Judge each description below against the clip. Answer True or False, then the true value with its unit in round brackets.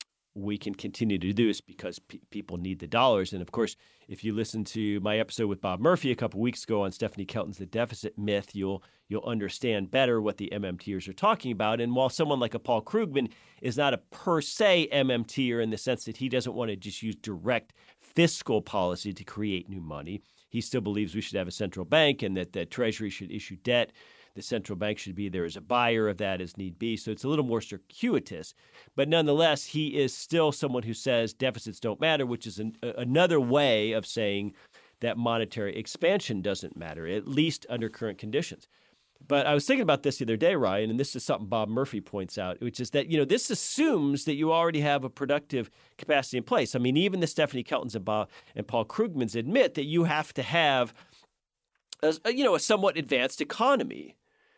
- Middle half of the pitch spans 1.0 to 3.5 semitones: False (5.4 semitones)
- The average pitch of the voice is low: True (115 Hz)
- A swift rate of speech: True (215 wpm)